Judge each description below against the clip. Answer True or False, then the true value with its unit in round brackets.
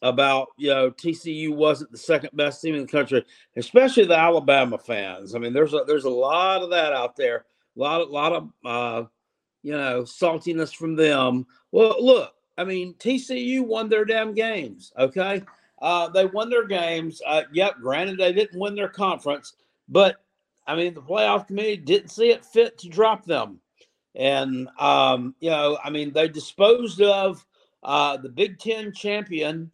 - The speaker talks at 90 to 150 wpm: False (180 wpm)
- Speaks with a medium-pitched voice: True (170 Hz)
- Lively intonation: True (6.4 semitones)